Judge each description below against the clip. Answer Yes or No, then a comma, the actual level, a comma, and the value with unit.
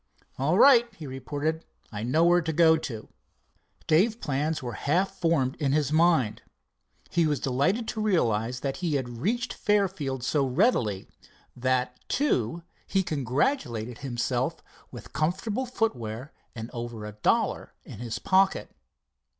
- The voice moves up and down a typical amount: No, wide, 6.4 semitones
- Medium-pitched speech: Yes, medium, 145 Hz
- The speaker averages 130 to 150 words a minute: Yes, slow, 135 wpm